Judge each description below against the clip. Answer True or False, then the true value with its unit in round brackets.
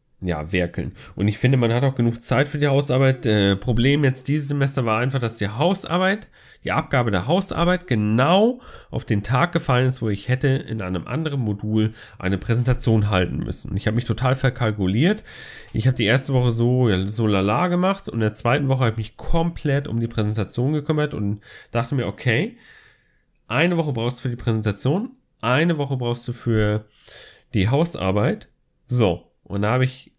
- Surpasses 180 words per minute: True (190 wpm)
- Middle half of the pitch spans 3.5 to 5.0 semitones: True (4.7 semitones)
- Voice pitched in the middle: False (125 Hz)